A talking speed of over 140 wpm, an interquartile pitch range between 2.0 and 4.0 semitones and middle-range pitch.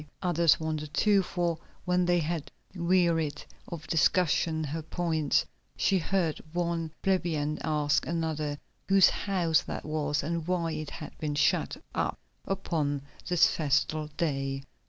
No: slow, 135 wpm; narrow, 2.5 semitones; medium, 160 Hz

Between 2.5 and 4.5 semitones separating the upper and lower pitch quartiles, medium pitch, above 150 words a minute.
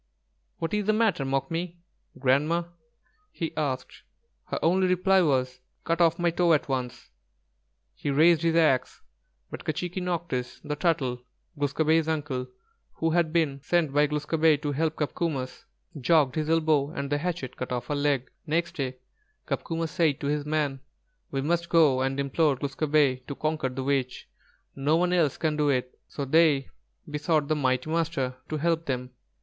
Yes: average, 3.4 semitones; medium, 150 Hz; average, 165 wpm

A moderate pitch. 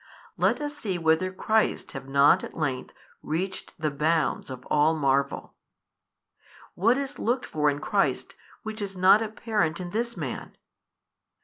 Yes: medium, 175 Hz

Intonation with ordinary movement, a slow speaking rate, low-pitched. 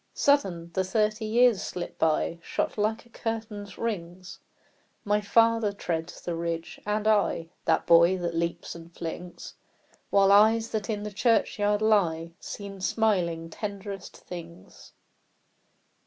No: average, 4.2 semitones; slow, 130 wpm; high, 200 Hz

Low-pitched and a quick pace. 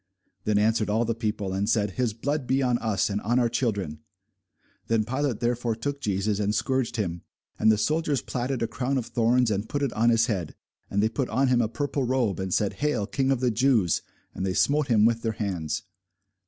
Yes: low, 115 Hz; fast, 220 wpm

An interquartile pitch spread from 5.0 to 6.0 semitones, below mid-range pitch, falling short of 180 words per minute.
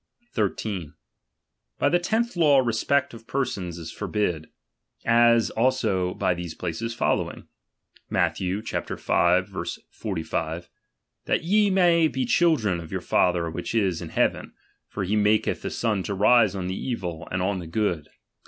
Yes: wide, 5.6 semitones; low, 105 Hz; average, 165 wpm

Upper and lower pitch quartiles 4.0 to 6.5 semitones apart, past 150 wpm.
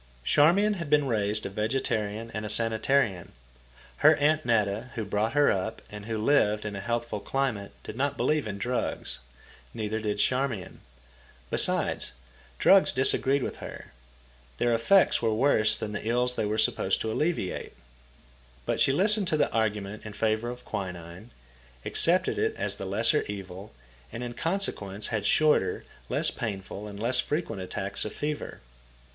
Yes: average, 4.5 semitones; average, 160 wpm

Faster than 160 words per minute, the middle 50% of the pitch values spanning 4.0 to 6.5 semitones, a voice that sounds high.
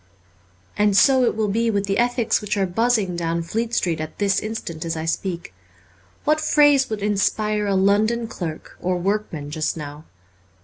Yes: average, 175 wpm; average, 4.7 semitones; high, 200 Hz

